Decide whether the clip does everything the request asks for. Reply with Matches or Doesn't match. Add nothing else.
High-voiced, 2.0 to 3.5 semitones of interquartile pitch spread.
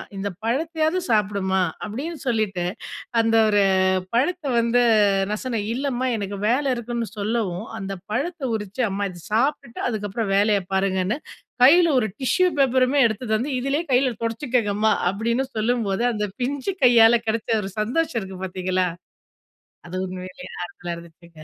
Doesn't match